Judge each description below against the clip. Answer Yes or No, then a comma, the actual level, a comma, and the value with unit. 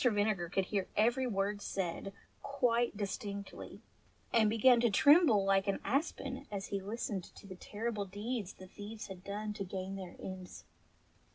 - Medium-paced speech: Yes, average, 165 wpm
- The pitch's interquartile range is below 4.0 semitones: Yes, average, 3.1 semitones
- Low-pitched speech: No, high, 205 Hz